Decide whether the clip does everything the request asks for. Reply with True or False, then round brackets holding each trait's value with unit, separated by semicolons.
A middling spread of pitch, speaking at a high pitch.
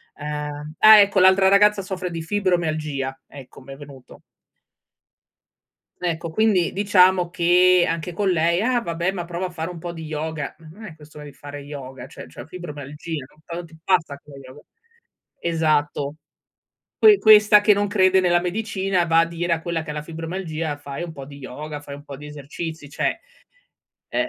False (3.8 semitones; 165 Hz)